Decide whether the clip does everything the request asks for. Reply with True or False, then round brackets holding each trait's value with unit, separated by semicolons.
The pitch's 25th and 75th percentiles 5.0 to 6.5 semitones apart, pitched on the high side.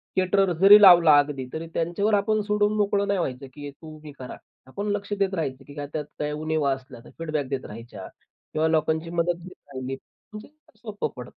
False (5.5 semitones; 160 Hz)